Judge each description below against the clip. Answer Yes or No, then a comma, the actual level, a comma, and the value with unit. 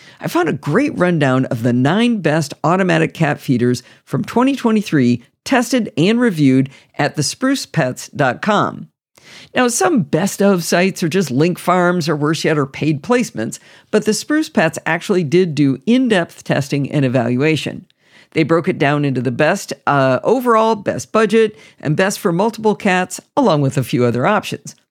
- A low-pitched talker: No, medium, 170 Hz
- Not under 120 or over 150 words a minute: No, average, 165 wpm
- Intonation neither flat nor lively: No, wide, 7.3 semitones